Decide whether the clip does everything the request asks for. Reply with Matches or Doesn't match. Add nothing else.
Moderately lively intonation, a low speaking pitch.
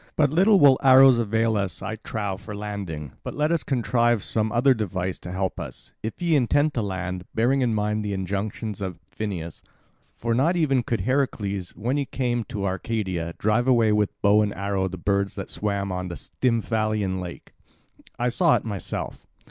Matches